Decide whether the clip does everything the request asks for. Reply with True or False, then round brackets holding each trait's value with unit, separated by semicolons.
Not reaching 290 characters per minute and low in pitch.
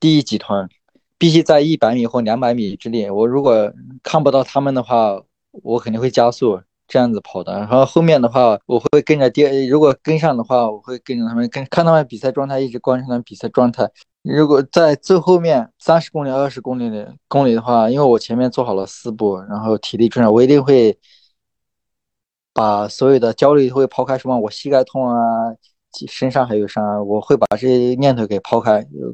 False (310 characters per minute; 125 Hz)